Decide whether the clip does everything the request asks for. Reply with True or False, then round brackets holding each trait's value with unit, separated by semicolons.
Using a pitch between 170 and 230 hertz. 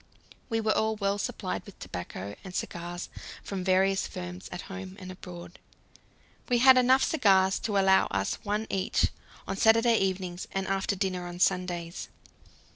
True (190 Hz)